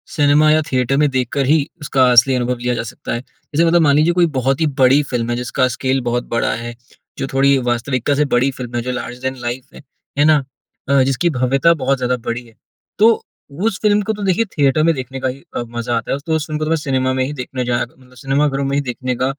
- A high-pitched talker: No, low, 135 Hz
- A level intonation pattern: No, average, 3.0 semitones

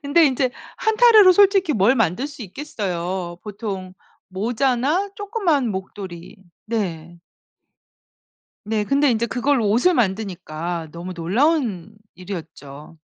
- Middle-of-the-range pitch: No, high, 220 Hz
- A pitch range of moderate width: No, wide, 7.8 semitones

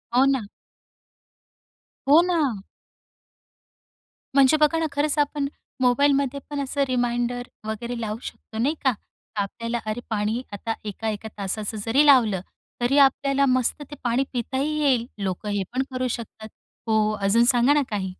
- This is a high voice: Yes, high, 245 Hz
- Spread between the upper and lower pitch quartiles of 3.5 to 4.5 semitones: Yes, average, 4.2 semitones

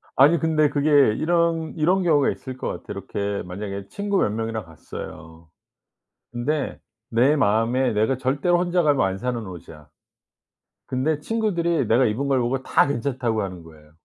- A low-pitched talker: Yes, low, 130 Hz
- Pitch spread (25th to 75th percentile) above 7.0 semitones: No, wide, 6.7 semitones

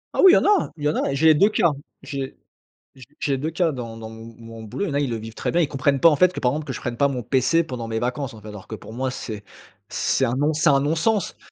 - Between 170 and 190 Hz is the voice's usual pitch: No, low, 135 Hz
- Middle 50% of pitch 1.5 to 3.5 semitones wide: No, average, 5.1 semitones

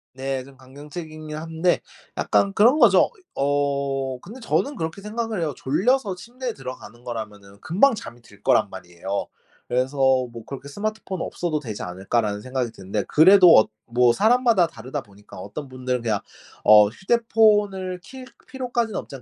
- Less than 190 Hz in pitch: Yes, medium, 140 Hz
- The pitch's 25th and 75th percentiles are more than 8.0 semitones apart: Yes, wide, 8.7 semitones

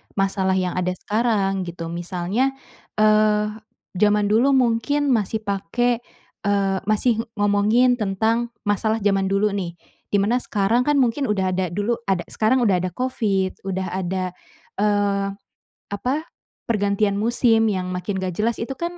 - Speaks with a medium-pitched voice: No, high, 205 Hz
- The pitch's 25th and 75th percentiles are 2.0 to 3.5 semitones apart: Yes, average, 3.2 semitones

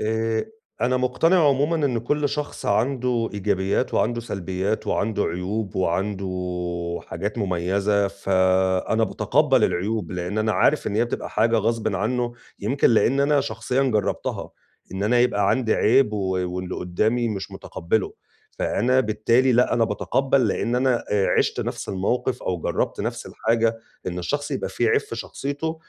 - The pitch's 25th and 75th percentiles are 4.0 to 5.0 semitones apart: Yes, average, 4.3 semitones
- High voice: No, low, 110 Hz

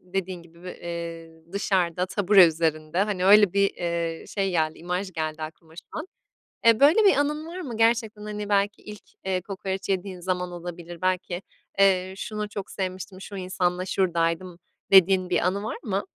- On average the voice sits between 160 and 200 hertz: Yes, medium, 185 Hz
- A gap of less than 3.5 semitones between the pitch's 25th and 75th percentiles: Yes, average, 2.8 semitones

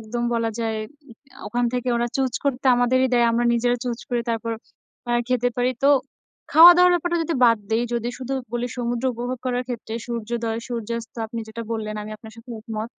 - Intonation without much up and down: Yes, narrow, 1.5 semitones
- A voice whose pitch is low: No, high, 240 Hz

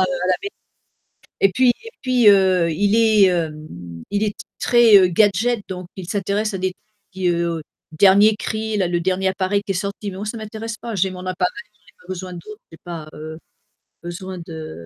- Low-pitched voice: No, high, 190 Hz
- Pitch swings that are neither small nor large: Yes, average, 3.3 semitones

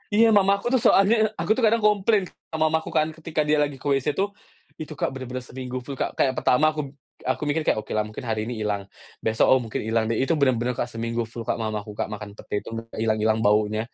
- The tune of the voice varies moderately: No, wide, 6.0 semitones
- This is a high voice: No, low, 125 Hz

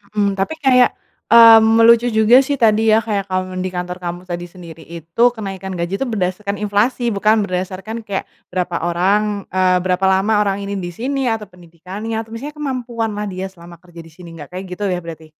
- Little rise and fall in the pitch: No, average, 3.7 semitones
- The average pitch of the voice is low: No, high, 195 Hz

